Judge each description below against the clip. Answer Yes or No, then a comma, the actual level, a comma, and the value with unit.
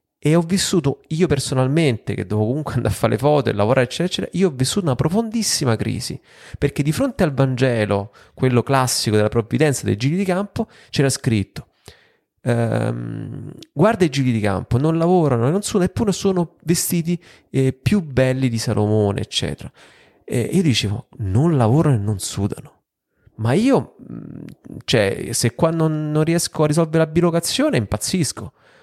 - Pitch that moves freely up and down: Yes, wide, 6.2 semitones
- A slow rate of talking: No, average, 165 wpm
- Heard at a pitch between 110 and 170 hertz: Yes, medium, 140 Hz